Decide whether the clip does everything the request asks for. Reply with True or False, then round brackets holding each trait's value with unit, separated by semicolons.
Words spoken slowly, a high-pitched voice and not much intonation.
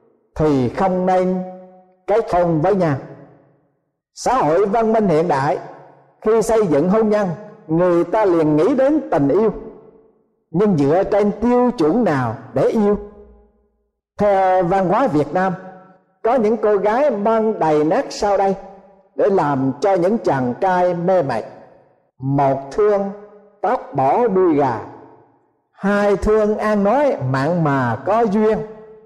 False (140 wpm; 195 Hz; 4.0 semitones)